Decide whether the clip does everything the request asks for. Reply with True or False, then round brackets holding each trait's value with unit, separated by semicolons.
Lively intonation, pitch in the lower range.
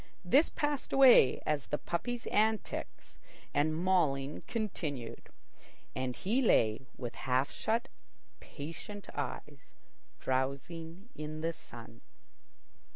False (7.6 semitones; 155 Hz)